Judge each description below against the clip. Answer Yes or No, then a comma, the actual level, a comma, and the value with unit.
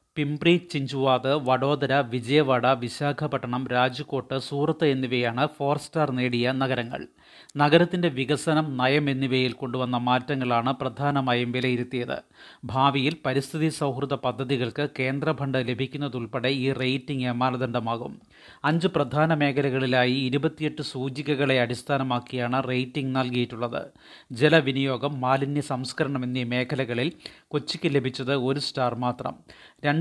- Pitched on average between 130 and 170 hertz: Yes, low, 135 Hz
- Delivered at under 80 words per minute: No, average, 95 wpm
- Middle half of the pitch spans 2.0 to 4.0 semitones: Yes, narrow, 2.4 semitones